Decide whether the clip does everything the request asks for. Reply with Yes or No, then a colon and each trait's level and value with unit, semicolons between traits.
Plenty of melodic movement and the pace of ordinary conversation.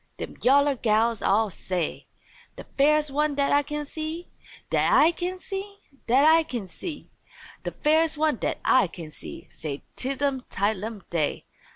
Yes: wide, 6.2 semitones; average, 160 wpm